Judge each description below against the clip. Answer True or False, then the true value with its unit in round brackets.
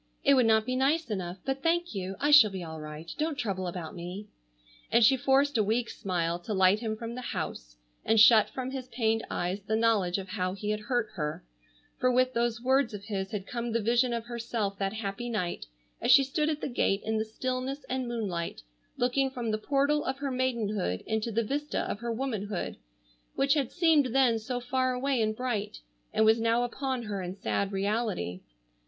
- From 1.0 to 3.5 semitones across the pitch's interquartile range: False (4.4 semitones)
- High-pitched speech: True (230 Hz)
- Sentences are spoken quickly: True (210 wpm)